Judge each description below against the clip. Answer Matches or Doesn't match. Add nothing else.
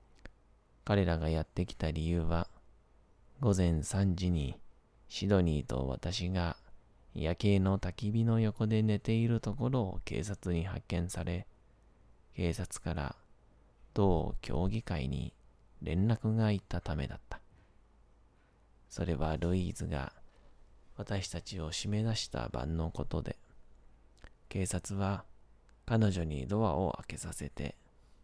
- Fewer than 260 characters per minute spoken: Matches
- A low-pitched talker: Matches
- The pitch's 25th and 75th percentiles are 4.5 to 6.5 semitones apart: Doesn't match